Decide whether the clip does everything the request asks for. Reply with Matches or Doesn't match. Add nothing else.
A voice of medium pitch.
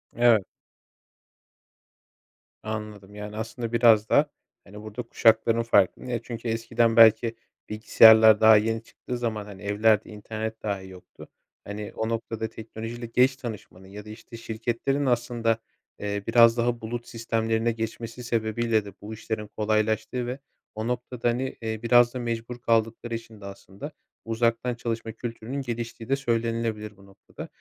Doesn't match